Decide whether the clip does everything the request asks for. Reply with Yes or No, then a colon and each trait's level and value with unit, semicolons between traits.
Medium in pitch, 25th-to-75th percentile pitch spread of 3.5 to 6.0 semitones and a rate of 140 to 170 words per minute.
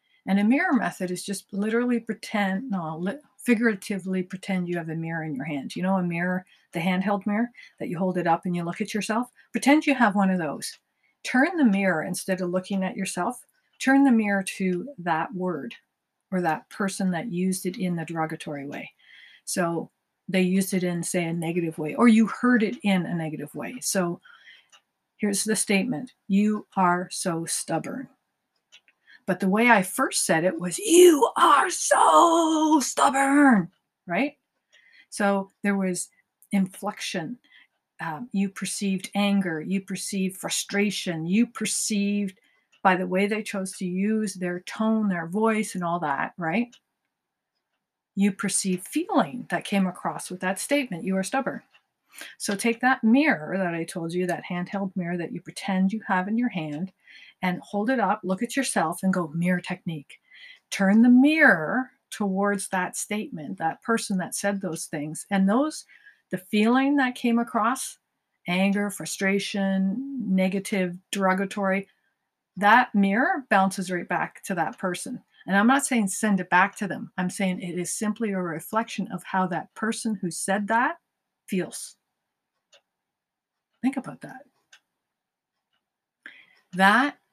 No: high, 195 Hz; average, 3.8 semitones; average, 160 wpm